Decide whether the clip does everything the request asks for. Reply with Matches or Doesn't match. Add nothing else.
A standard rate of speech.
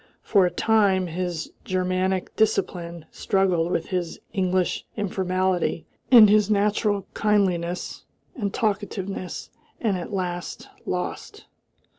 Doesn't match